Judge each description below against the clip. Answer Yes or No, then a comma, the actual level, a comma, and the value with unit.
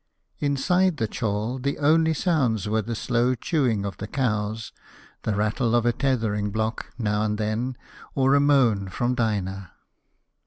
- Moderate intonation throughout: Yes, average, 4.1 semitones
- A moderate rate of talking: Yes, average, 155 wpm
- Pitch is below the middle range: Yes, low, 115 Hz